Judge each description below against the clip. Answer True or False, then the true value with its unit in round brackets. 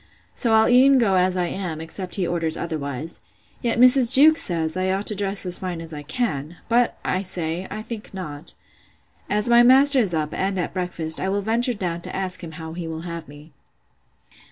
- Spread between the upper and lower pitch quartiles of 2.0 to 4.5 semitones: False (5.2 semitones)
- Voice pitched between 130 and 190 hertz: True (185 Hz)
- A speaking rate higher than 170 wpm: True (205 wpm)